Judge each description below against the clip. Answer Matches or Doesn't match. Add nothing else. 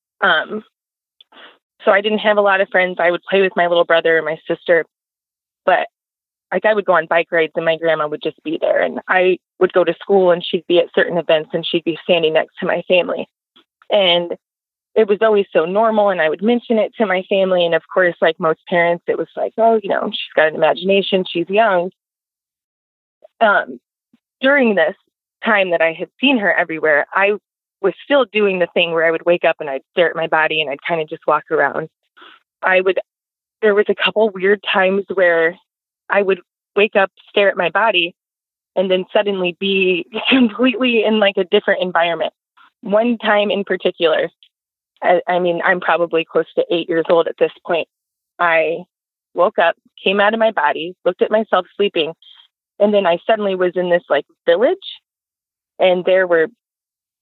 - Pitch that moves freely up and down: Doesn't match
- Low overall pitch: Doesn't match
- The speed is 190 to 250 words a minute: Matches